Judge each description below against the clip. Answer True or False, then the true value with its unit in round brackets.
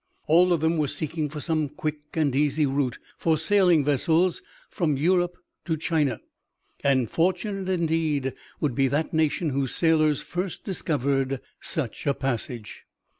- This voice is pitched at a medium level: True (155 Hz)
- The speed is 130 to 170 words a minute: True (145 wpm)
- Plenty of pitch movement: False (3.3 semitones)